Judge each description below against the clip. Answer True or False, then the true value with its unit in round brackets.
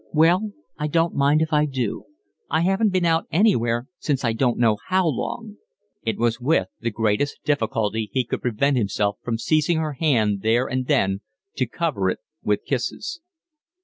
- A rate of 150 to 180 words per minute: True (175 wpm)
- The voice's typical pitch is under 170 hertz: True (135 Hz)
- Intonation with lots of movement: True (6.0 semitones)